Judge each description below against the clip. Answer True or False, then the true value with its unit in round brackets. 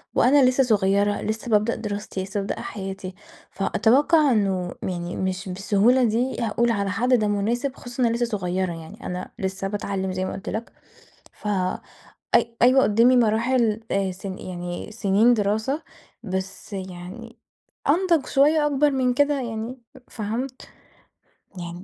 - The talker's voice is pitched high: True (215 Hz)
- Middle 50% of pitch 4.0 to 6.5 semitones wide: True (4.4 semitones)